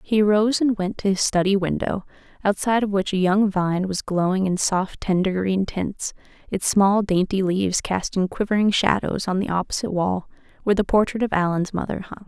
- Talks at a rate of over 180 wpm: Yes, average, 190 wpm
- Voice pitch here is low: No, high, 195 Hz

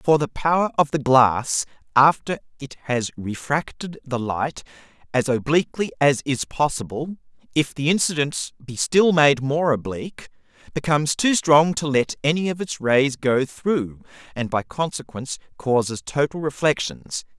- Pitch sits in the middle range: Yes, medium, 145 Hz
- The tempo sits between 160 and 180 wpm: No, average, 145 wpm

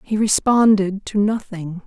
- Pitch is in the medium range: No, high, 205 Hz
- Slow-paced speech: Yes, slow, 130 wpm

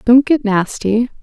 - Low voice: No, high, 235 Hz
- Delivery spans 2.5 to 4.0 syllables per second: Yes, 3.9 syllables/s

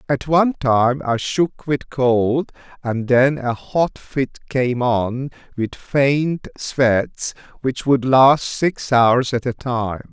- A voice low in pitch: Yes, low, 130 Hz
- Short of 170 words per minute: Yes, average, 150 wpm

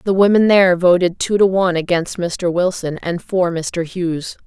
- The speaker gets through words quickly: No, average, 190 wpm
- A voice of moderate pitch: Yes, medium, 180 Hz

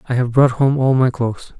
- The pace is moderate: No, fast, 265 wpm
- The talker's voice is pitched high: No, low, 125 Hz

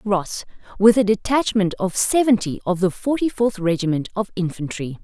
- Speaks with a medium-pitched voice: No, high, 200 Hz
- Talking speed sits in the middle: Yes, average, 155 wpm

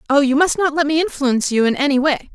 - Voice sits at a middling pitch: No, very high, 285 Hz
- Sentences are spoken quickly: Yes, fast, 280 wpm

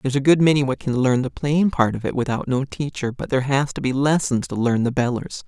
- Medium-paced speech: No, fast, 275 wpm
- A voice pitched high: No, low, 135 Hz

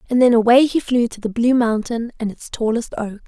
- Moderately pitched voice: No, high, 235 Hz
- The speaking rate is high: Yes, fast, 240 wpm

